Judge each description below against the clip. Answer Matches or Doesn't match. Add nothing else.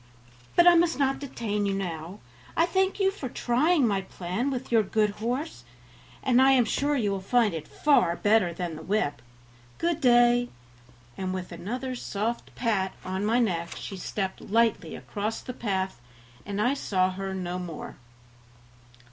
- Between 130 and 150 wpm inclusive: Doesn't match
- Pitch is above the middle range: Matches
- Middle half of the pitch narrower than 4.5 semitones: Doesn't match